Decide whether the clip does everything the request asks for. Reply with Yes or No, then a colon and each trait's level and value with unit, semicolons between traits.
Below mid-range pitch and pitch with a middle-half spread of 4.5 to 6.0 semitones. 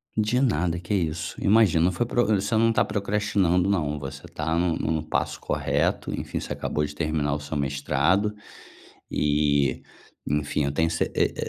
Yes: very low, 80 Hz; wide, 5.5 semitones